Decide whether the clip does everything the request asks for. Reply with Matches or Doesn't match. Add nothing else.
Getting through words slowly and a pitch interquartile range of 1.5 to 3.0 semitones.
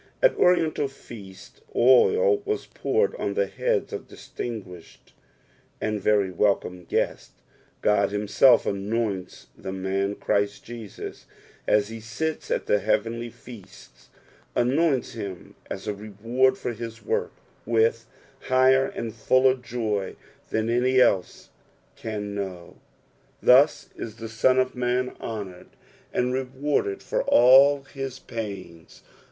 Doesn't match